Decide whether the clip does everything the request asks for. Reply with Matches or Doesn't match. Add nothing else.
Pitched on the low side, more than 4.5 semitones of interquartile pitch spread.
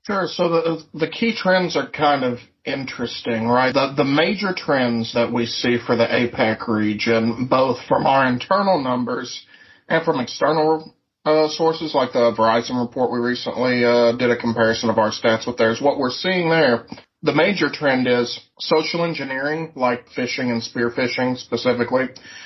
Matches